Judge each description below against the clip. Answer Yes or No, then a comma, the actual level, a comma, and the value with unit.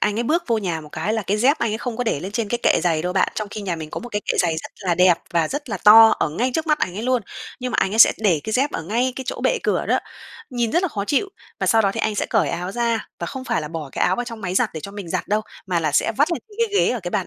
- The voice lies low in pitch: No, high, 215 Hz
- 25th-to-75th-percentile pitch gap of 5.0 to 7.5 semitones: Yes, wide, 5.4 semitones